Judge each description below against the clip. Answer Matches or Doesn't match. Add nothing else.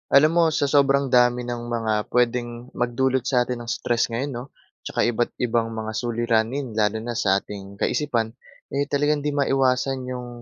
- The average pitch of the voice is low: Matches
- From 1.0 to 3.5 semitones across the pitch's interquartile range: Matches